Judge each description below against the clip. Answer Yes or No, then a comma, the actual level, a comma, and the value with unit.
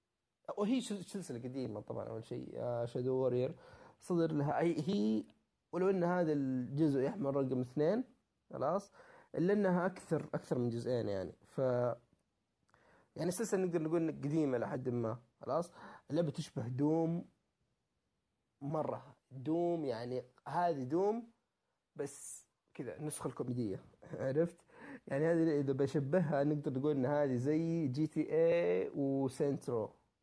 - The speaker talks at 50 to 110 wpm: No, average, 125 wpm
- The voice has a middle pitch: Yes, medium, 150 Hz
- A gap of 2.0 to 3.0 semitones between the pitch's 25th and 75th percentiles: No, average, 5.0 semitones